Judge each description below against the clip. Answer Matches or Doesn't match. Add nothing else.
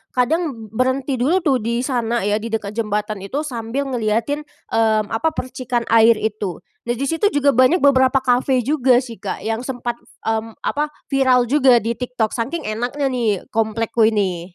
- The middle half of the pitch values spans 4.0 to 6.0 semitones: Doesn't match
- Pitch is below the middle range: Doesn't match